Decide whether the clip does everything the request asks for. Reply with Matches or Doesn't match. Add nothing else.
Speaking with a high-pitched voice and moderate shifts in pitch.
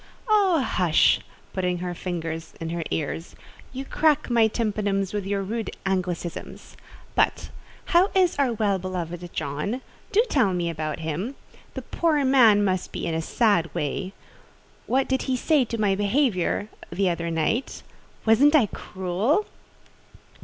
Doesn't match